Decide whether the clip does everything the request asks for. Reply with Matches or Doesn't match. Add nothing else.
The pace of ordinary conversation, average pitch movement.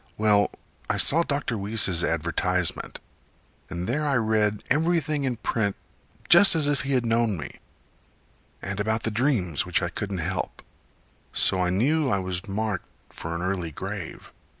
Doesn't match